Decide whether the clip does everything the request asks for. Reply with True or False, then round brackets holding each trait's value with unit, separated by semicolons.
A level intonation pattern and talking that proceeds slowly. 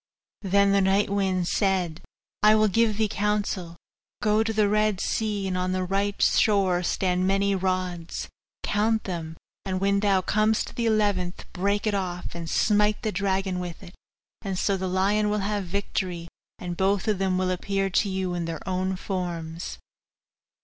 False (2.2 semitones; 175 wpm)